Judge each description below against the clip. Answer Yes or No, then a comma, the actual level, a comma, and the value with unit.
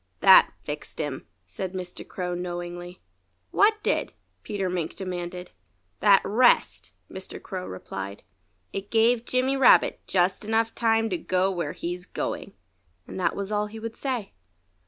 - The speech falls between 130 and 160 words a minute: Yes, average, 145 wpm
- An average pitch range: Yes, average, 4.0 semitones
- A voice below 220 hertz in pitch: Yes, high, 190 Hz